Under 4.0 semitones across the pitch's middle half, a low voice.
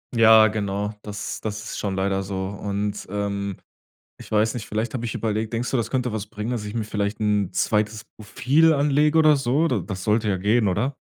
Yes: narrow, 2.6 semitones; low, 110 Hz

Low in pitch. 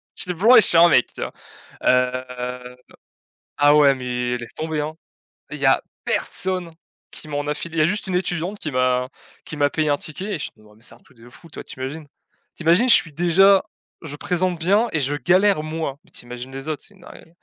No: medium, 150 Hz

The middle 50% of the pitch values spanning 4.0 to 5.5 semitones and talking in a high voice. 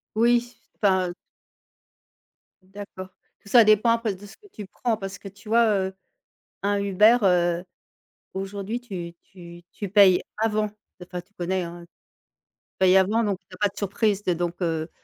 No: average, 2.8 semitones; high, 195 Hz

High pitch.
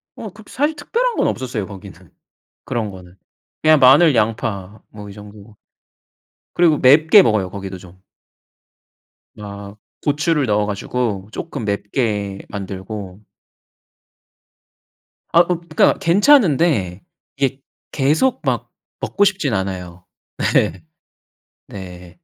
No: low, 110 Hz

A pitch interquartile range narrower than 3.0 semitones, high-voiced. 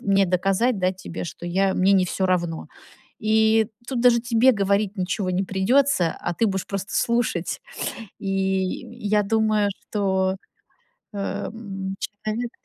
Yes: narrow, 2.6 semitones; high, 195 Hz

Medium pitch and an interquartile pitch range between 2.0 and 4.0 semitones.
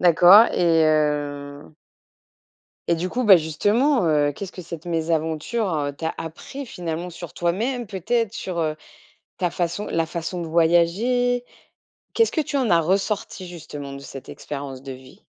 No: medium, 170 Hz; average, 4.6 semitones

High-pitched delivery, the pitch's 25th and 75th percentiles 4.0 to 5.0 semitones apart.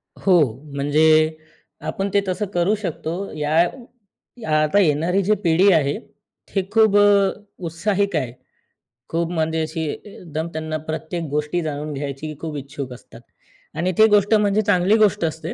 No: medium, 165 Hz; average, 4.4 semitones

